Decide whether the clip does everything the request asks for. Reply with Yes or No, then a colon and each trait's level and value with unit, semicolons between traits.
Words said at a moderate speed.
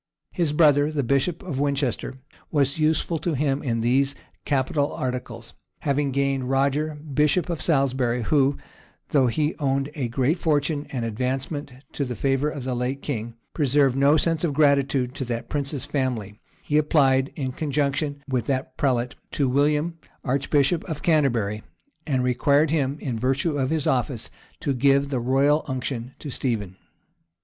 Yes: average, 155 wpm